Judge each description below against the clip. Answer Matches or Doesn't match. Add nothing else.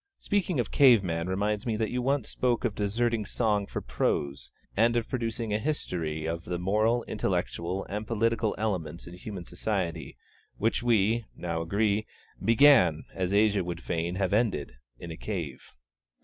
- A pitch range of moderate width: Matches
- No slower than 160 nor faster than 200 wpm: Matches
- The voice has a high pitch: Doesn't match